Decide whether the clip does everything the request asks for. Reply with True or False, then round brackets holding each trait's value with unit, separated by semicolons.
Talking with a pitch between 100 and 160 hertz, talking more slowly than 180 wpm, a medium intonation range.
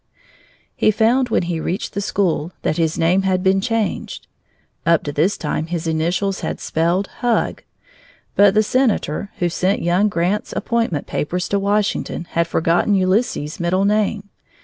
False (185 Hz; 155 wpm; 3.6 semitones)